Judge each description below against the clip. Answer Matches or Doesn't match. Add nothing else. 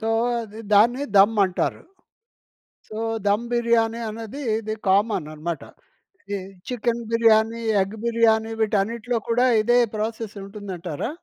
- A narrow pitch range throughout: Matches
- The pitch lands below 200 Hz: Doesn't match